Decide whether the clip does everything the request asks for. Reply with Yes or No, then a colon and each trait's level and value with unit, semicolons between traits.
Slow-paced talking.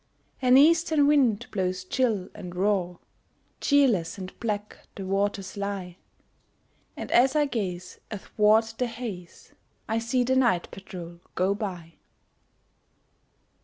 Yes: slow, 120 wpm